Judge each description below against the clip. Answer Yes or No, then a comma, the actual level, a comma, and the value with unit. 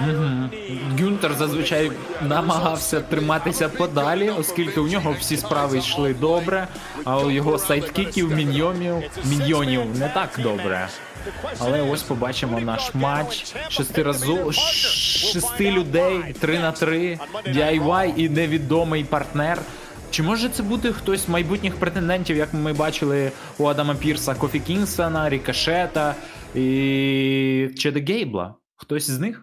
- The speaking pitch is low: No, medium, 155 Hz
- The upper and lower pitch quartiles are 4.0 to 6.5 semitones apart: No, average, 3.4 semitones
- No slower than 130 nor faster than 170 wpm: No, average, 120 wpm